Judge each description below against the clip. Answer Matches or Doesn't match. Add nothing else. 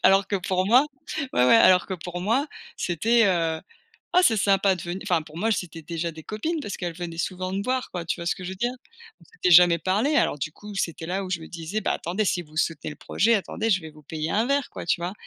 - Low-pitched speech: Doesn't match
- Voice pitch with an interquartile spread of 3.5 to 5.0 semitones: Matches